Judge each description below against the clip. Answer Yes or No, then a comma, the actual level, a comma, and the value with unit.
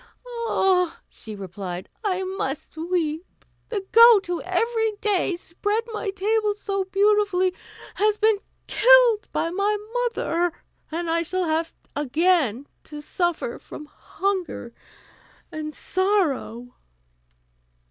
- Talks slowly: Yes, slow, 110 wpm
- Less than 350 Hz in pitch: No, very high, 370 Hz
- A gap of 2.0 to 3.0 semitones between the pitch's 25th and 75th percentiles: No, average, 4.8 semitones